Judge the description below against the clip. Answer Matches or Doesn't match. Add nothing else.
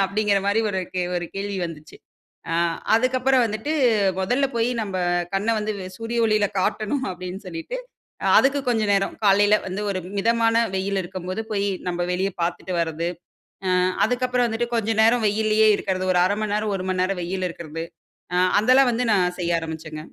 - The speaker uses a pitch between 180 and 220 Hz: Matches